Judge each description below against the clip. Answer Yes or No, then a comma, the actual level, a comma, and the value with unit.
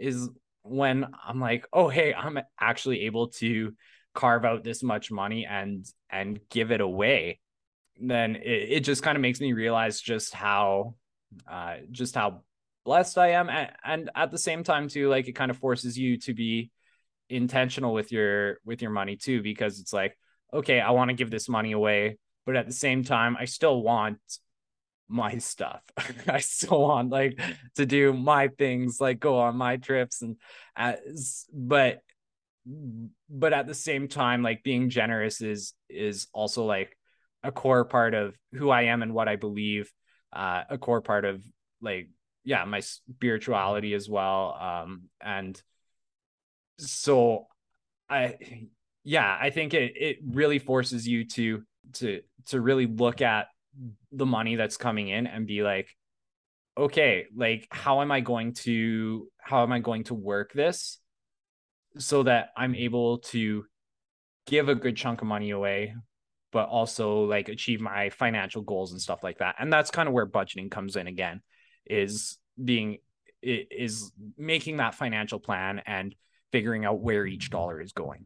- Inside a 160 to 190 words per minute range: Yes, average, 170 wpm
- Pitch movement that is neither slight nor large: Yes, average, 3.5 semitones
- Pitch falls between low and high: No, low, 120 Hz